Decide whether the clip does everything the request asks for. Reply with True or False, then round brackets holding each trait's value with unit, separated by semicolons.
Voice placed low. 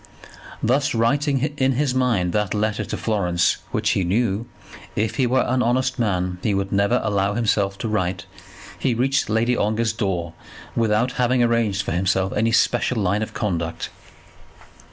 True (110 Hz)